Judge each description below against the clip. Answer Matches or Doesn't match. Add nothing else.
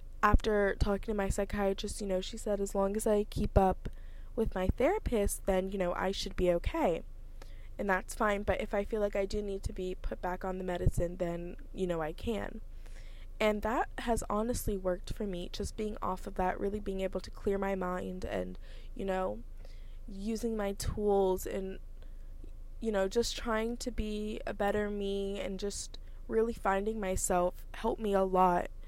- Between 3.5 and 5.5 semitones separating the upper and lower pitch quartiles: Doesn't match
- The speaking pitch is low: Doesn't match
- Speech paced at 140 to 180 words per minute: Doesn't match